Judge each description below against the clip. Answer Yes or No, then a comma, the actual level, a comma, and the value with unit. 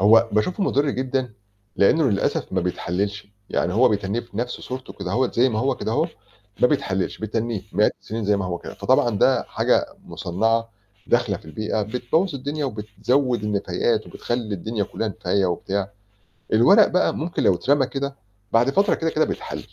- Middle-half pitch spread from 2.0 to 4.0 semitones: No, average, 4.6 semitones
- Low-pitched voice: Yes, low, 115 Hz